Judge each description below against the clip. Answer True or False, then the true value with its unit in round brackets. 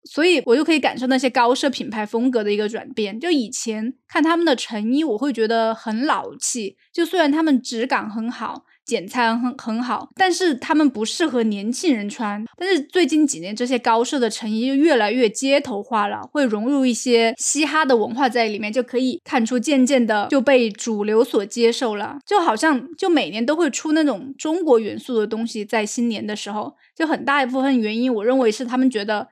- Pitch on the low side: False (250 Hz)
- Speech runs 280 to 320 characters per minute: True (310 characters per minute)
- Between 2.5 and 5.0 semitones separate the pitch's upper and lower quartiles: True (4.3 semitones)